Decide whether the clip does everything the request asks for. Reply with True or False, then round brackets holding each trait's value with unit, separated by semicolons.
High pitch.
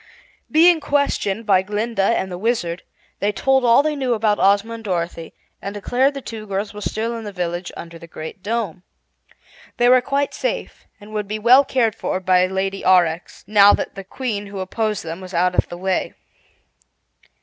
True (205 Hz)